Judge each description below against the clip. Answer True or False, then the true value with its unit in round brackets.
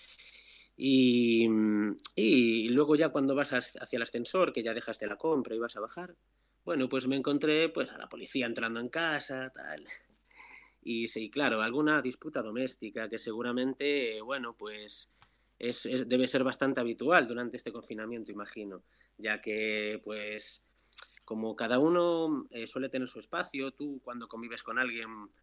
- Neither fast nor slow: True (160 wpm)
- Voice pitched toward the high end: False (120 Hz)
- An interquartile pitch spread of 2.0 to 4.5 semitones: True (3.3 semitones)